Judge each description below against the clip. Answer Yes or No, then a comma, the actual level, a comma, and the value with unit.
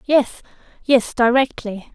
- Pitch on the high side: Yes, high, 245 Hz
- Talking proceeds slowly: Yes, slow, 90 wpm